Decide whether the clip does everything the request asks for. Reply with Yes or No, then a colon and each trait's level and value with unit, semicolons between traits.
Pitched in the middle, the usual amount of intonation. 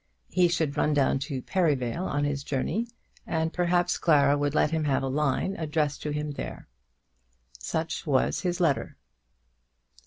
Yes: medium, 150 Hz; average, 3.0 semitones